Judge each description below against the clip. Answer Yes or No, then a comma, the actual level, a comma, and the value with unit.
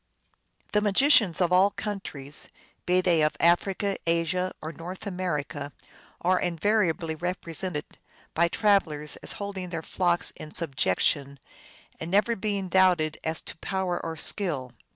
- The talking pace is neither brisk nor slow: No, slow, 130 wpm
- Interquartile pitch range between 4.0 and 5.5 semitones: No, average, 3.2 semitones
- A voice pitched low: No, medium, 175 Hz